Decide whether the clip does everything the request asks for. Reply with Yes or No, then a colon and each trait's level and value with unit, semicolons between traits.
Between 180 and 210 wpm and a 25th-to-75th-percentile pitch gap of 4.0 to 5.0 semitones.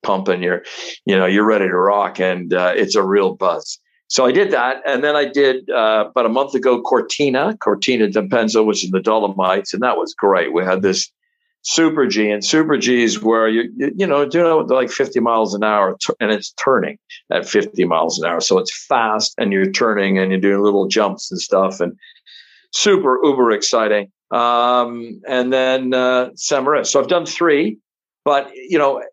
No: average, 200 wpm; wide, 5.4 semitones